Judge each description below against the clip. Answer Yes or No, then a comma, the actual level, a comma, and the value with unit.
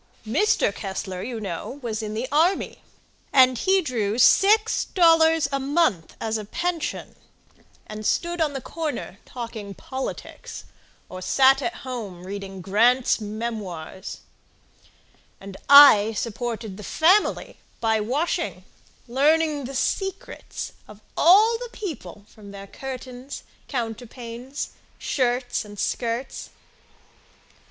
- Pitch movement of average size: No, wide, 6.0 semitones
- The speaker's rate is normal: No, slow, 115 wpm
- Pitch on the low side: No, high, 245 Hz